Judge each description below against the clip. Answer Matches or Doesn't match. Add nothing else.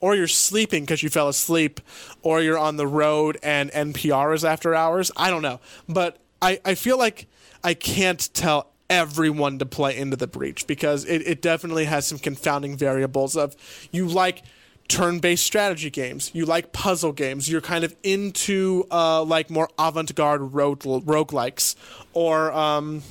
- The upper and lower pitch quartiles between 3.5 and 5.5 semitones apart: Doesn't match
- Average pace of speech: Matches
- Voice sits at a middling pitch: Matches